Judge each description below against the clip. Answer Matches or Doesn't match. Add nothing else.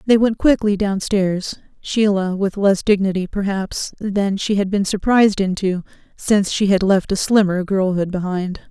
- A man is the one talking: Doesn't match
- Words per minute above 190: Doesn't match